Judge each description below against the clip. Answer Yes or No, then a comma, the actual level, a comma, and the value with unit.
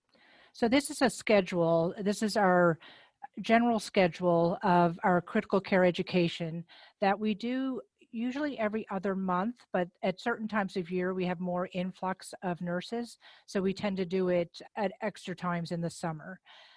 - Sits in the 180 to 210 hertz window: Yes, high, 190 Hz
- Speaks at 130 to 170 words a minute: Yes, average, 165 wpm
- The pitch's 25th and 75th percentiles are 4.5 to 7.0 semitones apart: No, average, 3.6 semitones